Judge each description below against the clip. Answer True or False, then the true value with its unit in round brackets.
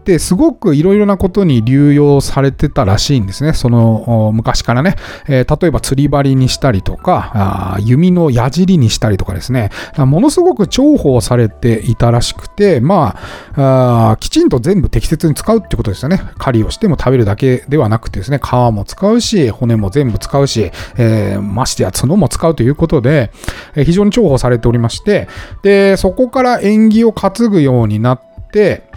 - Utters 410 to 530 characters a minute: False (360 characters per minute)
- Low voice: True (130 Hz)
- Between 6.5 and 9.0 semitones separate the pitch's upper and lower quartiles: True (8.1 semitones)